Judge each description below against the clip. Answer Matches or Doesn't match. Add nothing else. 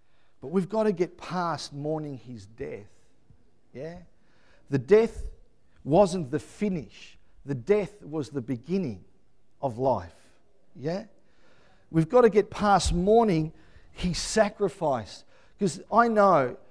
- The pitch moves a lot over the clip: Matches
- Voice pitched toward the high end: Doesn't match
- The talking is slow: Matches